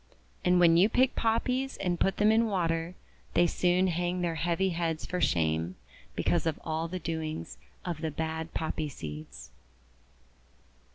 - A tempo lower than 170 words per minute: Yes, average, 155 wpm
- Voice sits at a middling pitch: Yes, medium, 170 Hz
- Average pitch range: No, narrow, 2.3 semitones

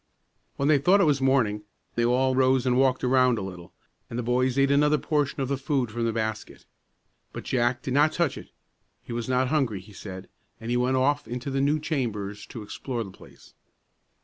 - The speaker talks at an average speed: No, fast, 210 wpm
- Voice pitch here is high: No, low, 130 Hz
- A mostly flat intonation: No, average, 3.0 semitones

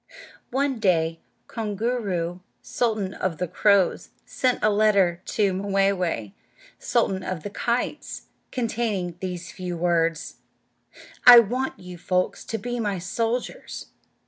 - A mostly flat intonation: No, average, 4.2 semitones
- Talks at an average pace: No, slow, 120 wpm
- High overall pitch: Yes, high, 195 Hz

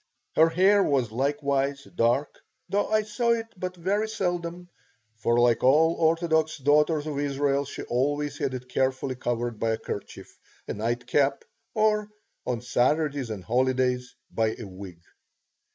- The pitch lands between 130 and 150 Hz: Yes, medium, 140 Hz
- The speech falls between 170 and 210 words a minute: No, average, 145 wpm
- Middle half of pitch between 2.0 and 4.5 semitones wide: No, average, 5.2 semitones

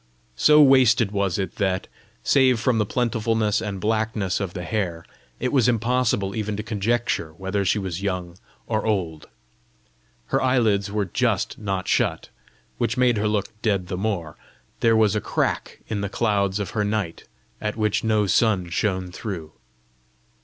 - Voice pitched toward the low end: Yes, low, 105 Hz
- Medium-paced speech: Yes, average, 160 wpm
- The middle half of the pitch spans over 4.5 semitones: No, average, 2.8 semitones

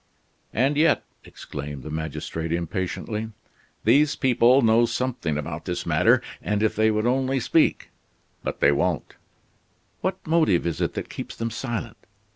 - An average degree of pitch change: No, wide, 7.5 semitones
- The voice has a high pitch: No, low, 110 Hz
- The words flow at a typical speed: Yes, average, 150 wpm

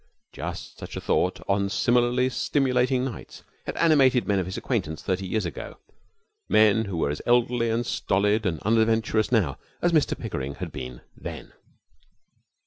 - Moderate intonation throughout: Yes, average, 4.3 semitones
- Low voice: Yes, low, 110 Hz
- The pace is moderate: Yes, average, 155 wpm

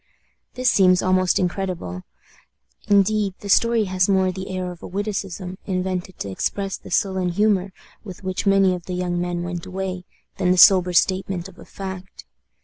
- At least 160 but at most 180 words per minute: Yes, average, 170 wpm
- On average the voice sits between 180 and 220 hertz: Yes, medium, 185 Hz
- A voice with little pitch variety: Yes, narrow, 1.4 semitones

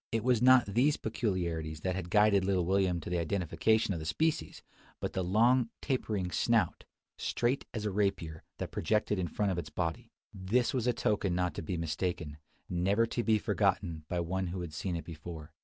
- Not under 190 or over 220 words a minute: Yes, average, 195 wpm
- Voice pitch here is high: No, very low, 95 Hz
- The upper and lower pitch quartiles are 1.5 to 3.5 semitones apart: No, average, 4.2 semitones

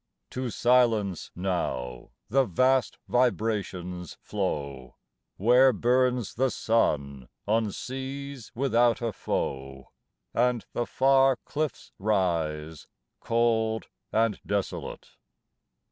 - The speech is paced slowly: Yes, slow, 90 wpm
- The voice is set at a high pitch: No, low, 110 Hz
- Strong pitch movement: Yes, wide, 5.8 semitones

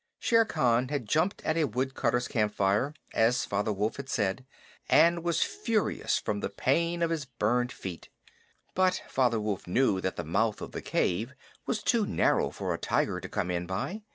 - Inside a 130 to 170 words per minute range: No, average, 180 wpm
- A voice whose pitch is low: Yes, low, 125 Hz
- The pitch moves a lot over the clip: Yes, wide, 7.9 semitones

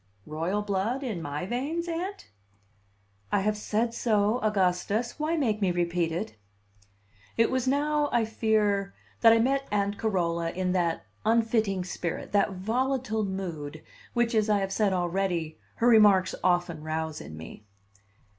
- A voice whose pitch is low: No, high, 205 Hz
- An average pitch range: Yes, average, 4.5 semitones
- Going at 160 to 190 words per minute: No, average, 145 wpm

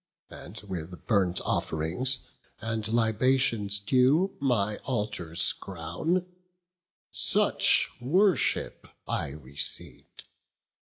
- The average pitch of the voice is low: Yes, low, 110 Hz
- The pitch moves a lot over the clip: Yes, wide, 6.2 semitones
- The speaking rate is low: Yes, slow, 75 wpm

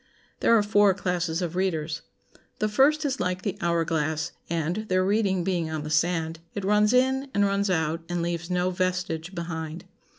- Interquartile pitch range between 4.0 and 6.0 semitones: No, average, 3.6 semitones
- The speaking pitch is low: No, medium, 180 Hz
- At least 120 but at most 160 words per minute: No, average, 185 wpm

